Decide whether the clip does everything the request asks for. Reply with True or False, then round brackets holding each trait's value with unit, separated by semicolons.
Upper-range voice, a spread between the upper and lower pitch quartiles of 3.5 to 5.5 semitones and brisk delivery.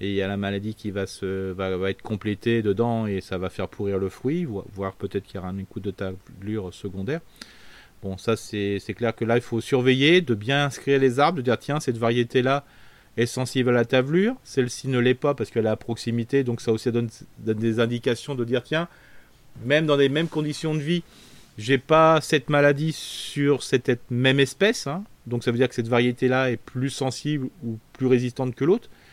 False (120 Hz; 4.3 semitones; 225 wpm)